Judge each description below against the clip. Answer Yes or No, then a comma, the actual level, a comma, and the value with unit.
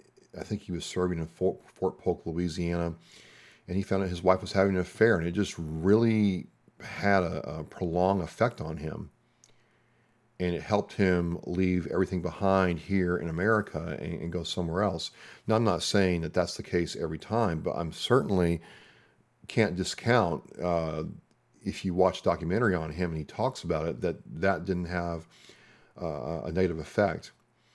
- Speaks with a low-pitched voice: Yes, very low, 90 Hz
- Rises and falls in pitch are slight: Yes, narrow, 2.3 semitones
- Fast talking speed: No, average, 175 wpm